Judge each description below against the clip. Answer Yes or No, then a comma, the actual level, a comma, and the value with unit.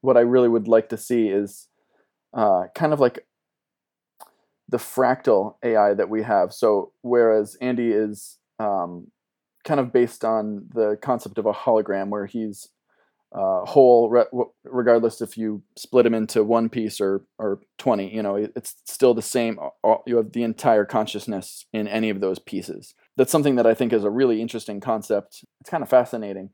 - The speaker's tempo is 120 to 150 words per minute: No, average, 175 wpm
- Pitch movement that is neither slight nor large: No, narrow, 2.3 semitones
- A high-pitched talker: No, low, 110 Hz